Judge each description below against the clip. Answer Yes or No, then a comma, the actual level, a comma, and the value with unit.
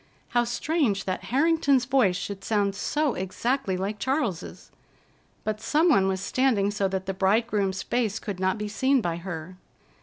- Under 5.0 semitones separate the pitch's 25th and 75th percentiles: No, average, 5.3 semitones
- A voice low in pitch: No, high, 205 Hz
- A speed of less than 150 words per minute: No, average, 160 wpm